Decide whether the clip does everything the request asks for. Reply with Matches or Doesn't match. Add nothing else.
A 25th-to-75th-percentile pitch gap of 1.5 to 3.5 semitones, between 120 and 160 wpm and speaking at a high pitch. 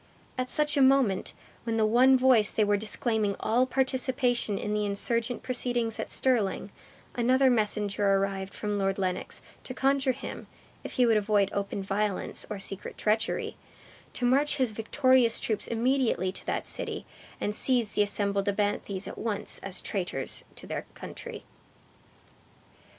Doesn't match